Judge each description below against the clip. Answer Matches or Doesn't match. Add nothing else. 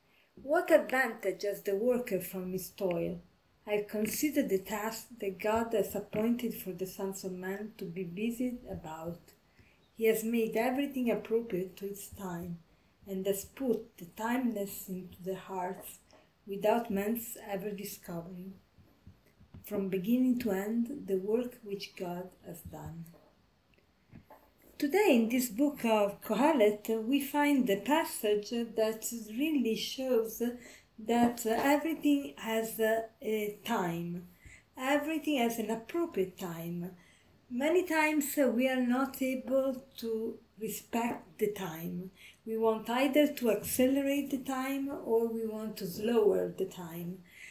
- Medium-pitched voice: Doesn't match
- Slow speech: Matches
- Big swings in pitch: Doesn't match